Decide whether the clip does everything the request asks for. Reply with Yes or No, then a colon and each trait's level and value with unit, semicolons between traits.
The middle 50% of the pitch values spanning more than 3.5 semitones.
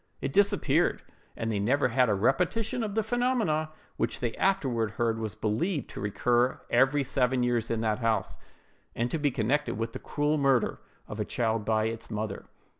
Yes: average, 4.7 semitones